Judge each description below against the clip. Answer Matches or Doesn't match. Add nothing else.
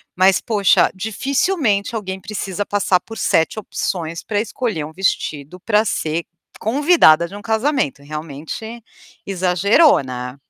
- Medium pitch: Doesn't match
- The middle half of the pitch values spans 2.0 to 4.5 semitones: Doesn't match